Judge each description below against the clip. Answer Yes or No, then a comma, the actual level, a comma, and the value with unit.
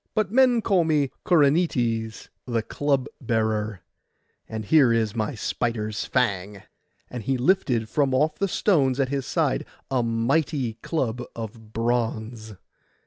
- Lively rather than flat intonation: No, average, 4.7 semitones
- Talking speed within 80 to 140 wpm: Yes, slow, 135 wpm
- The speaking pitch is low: Yes, low, 125 Hz